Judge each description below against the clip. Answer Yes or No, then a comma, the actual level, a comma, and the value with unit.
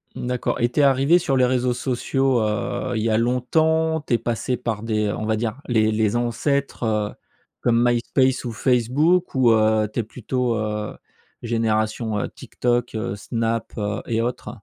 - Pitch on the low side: Yes, low, 120 Hz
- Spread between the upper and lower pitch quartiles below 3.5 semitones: Yes, average, 2.7 semitones